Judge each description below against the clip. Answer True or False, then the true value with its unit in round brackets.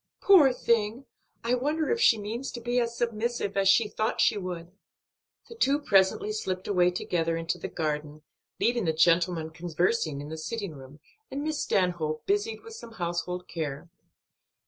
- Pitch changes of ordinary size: False (6.2 semitones)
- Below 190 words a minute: True (170 wpm)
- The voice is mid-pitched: False (195 Hz)